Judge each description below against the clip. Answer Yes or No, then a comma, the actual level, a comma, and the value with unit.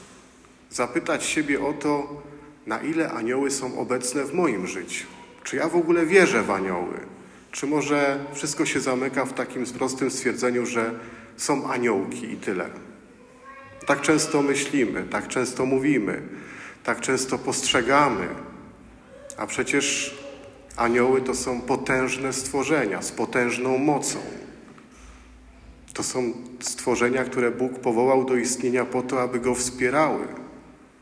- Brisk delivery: No, average, 125 wpm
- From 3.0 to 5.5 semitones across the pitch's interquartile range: No, narrow, 2.4 semitones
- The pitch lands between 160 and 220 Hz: No, low, 130 Hz